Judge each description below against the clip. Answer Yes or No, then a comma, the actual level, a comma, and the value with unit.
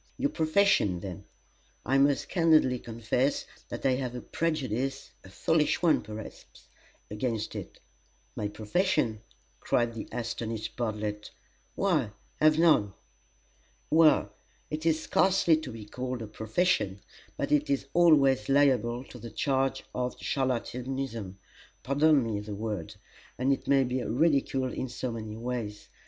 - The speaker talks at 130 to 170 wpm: Yes, average, 140 wpm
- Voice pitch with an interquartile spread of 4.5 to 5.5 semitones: Yes, average, 4.8 semitones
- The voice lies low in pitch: Yes, low, 125 Hz